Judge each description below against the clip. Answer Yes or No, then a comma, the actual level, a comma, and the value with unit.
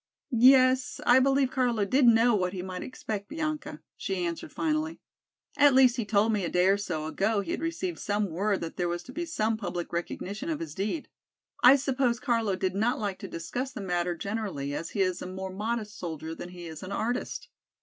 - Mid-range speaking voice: No, high, 210 Hz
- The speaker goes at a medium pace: No, fast, 210 wpm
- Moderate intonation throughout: No, wide, 5.9 semitones